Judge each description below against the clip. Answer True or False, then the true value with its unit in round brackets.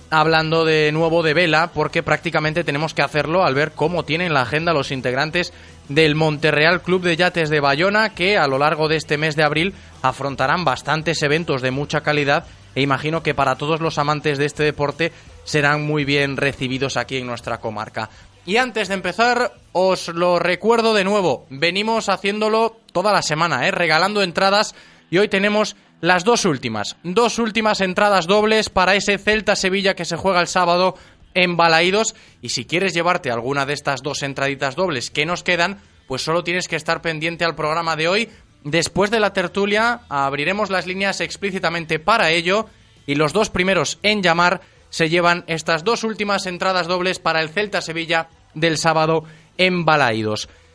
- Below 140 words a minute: False (175 wpm)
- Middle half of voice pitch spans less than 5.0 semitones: True (4.3 semitones)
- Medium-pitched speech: True (165 Hz)